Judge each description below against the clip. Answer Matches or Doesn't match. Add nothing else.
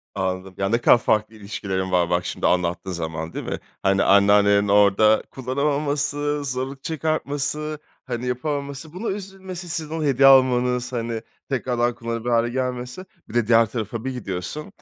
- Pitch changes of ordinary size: Doesn't match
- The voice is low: Matches